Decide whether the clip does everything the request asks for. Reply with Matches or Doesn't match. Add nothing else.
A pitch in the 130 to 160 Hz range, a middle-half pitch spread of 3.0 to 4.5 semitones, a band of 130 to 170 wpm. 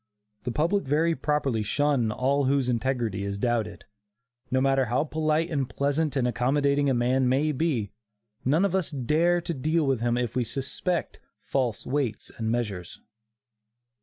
Matches